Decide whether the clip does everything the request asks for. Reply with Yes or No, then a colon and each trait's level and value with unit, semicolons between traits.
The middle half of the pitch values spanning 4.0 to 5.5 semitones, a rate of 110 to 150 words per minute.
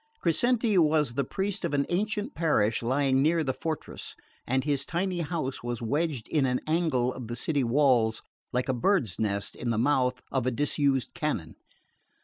No: average, 4.7 semitones; average, 175 wpm